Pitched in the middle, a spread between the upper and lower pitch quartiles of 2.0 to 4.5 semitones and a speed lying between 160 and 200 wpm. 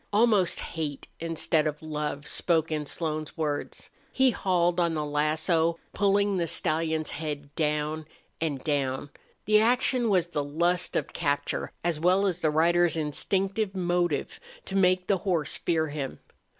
No: medium, 165 Hz; average, 3.3 semitones; average, 150 wpm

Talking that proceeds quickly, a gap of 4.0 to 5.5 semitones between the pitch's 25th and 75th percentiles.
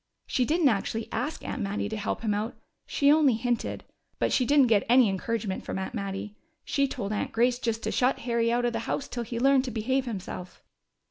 No: fast, 215 wpm; average, 3.4 semitones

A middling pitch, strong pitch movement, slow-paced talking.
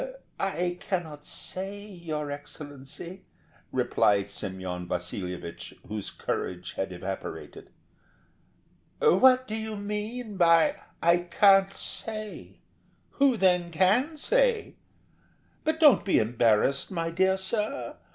Yes: medium, 180 Hz; wide, 7.5 semitones; slow, 105 wpm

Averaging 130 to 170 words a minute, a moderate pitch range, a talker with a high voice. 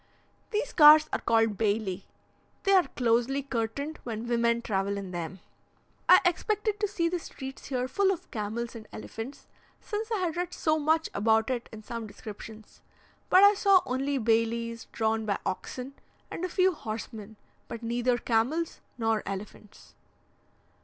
No: average, 155 wpm; wide, 6.4 semitones; high, 235 Hz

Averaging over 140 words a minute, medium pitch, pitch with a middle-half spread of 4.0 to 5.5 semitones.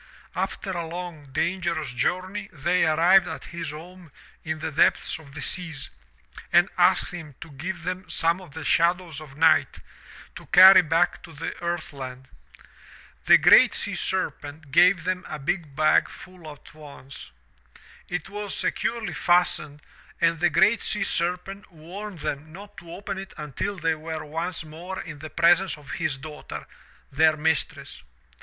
No: average, 160 wpm; medium, 165 Hz; average, 2.8 semitones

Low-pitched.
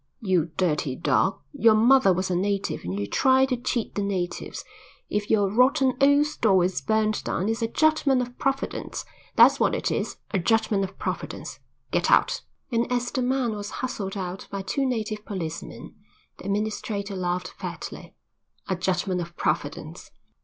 No: high, 210 Hz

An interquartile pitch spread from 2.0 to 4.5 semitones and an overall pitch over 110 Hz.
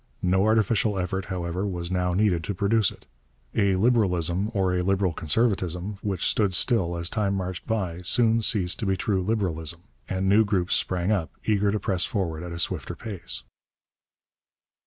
No: average, 2.8 semitones; very low, 95 Hz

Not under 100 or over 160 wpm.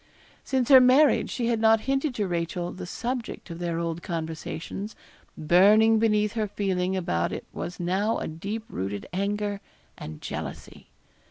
Yes: average, 155 wpm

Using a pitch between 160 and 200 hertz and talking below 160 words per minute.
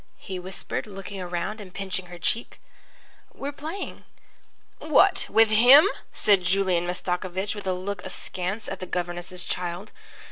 Yes: high, 190 Hz; average, 140 wpm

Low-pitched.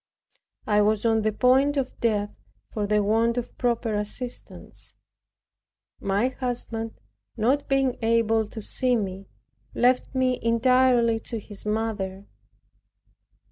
No: high, 230 Hz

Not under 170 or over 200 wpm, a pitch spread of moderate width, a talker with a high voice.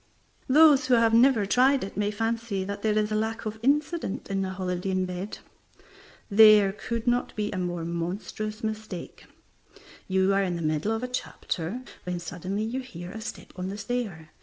Yes: average, 185 wpm; average, 3.6 semitones; high, 210 Hz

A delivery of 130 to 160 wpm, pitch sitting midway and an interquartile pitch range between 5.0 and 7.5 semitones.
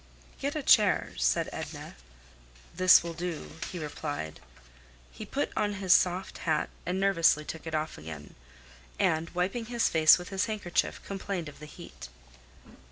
No: average, 155 wpm; medium, 170 Hz; average, 3.8 semitones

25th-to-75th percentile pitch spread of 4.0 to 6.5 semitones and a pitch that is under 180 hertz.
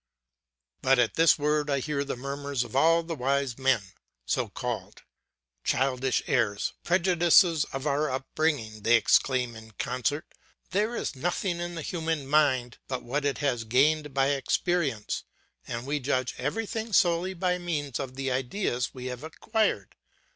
Yes: average, 4.3 semitones; medium, 140 Hz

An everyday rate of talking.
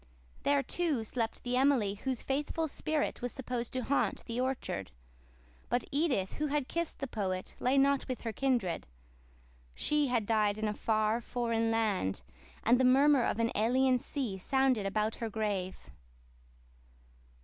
Yes: average, 155 wpm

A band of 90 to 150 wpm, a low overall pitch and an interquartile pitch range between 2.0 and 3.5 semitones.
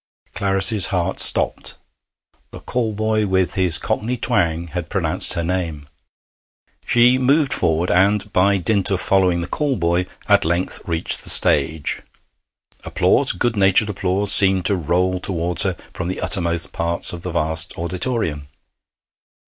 Yes: average, 145 wpm; very low, 90 Hz; average, 3.1 semitones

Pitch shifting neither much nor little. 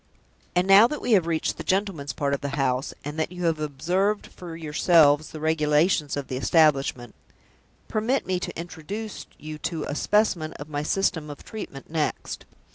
Yes: average, 3.9 semitones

